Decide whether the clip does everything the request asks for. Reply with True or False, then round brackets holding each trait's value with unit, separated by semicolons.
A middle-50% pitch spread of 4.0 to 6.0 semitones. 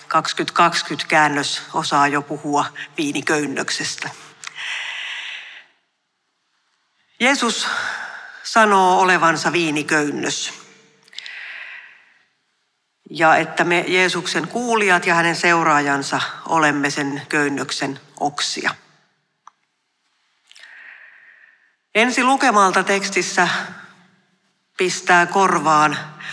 True (4.3 semitones)